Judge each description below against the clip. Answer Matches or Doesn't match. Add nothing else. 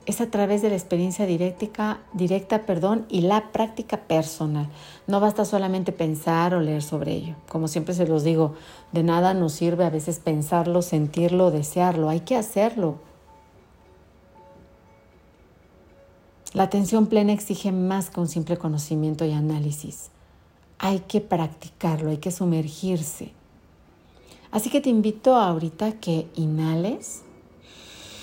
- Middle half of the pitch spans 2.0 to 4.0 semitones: Doesn't match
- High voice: Doesn't match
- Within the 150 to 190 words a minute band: Doesn't match